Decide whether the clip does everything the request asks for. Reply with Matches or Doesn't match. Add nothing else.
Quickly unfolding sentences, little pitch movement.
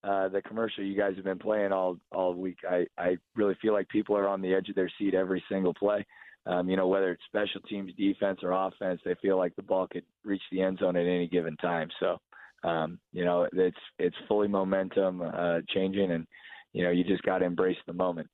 Matches